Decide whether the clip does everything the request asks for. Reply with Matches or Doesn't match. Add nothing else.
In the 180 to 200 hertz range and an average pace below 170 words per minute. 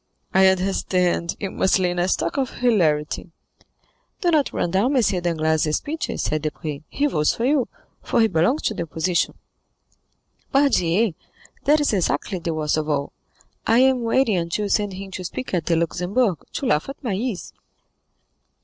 Doesn't match